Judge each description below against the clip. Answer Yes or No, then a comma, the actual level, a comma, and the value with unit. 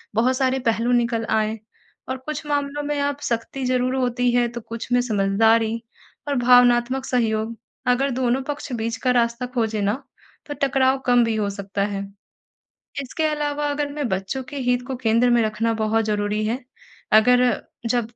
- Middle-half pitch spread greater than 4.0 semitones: No, average, 2.8 semitones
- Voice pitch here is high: Yes, high, 245 Hz